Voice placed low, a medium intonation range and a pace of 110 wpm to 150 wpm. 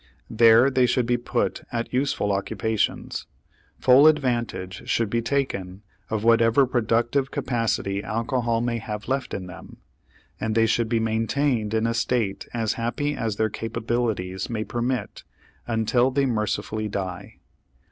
No: low, 115 Hz; narrow, 2.2 semitones; average, 140 wpm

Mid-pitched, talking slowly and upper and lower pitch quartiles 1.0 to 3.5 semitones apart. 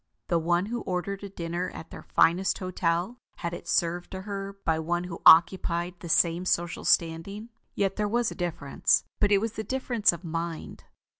No: medium, 180 Hz; average, 190 wpm; average, 2.9 semitones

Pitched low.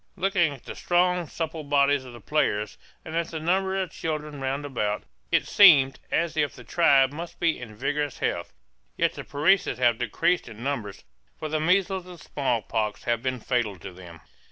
No: medium, 145 Hz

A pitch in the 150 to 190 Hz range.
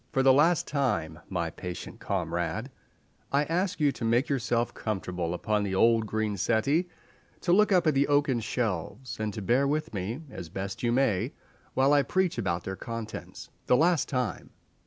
No: low, 115 Hz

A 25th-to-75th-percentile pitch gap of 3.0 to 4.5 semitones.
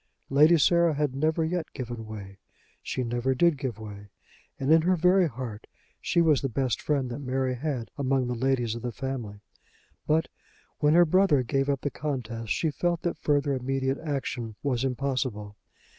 Yes: average, 4.1 semitones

